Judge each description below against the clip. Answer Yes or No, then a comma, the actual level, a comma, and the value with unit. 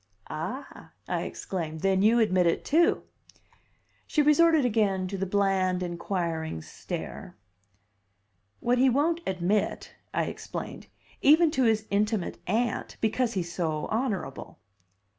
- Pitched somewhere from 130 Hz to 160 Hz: No, high, 205 Hz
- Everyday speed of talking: No, slow, 120 wpm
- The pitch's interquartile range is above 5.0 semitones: Yes, wide, 5.5 semitones